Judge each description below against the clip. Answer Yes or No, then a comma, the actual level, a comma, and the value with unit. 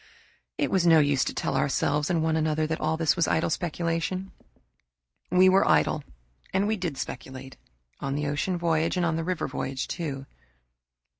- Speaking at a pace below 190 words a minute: Yes, average, 170 wpm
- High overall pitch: No, medium, 160 Hz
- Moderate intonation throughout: Yes, average, 3.1 semitones